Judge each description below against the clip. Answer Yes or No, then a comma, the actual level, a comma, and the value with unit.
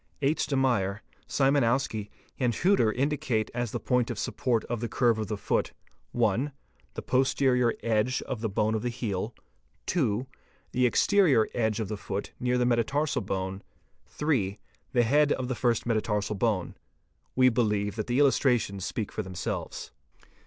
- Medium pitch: No, low, 120 Hz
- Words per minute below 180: Yes, average, 160 wpm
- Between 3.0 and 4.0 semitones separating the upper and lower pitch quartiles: Yes, average, 3.4 semitones